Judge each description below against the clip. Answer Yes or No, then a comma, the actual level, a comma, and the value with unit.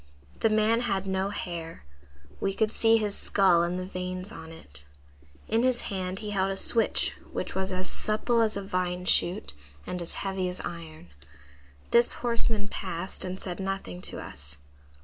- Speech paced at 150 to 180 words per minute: Yes, average, 170 wpm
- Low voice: No, high, 190 Hz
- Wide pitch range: No, average, 3.0 semitones